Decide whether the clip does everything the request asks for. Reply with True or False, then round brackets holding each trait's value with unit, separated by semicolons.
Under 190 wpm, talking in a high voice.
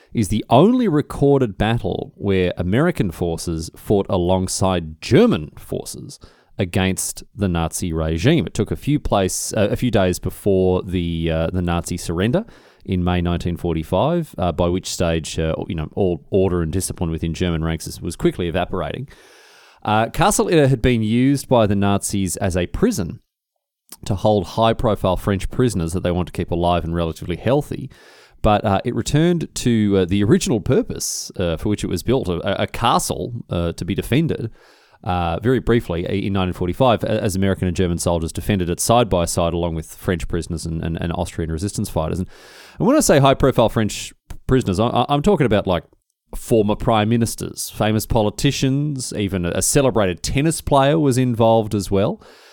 False (170 wpm; 100 Hz)